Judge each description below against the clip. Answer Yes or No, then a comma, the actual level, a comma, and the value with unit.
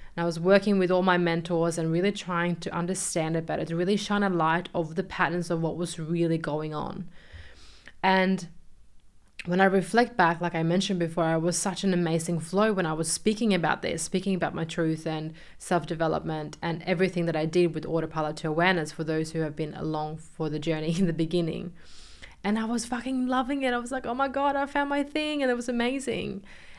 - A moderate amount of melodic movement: Yes, average, 3.2 semitones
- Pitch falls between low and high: Yes, medium, 175 Hz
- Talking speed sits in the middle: No, fast, 215 wpm